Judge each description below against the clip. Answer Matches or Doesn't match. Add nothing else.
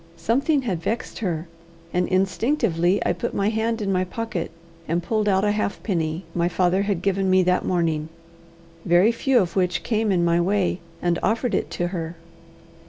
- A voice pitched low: Doesn't match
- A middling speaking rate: Matches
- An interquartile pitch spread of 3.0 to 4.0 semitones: Matches